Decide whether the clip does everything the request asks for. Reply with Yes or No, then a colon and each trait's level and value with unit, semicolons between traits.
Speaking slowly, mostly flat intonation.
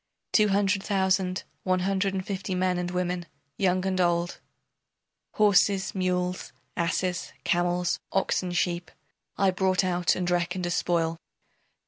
Yes: slow, 130 wpm; narrow, 1.3 semitones